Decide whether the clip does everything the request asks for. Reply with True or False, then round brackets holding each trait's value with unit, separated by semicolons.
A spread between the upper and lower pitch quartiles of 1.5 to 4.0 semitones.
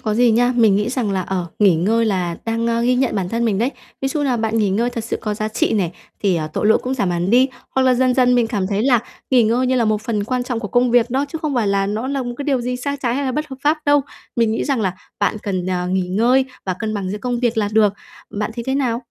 True (3.5 semitones)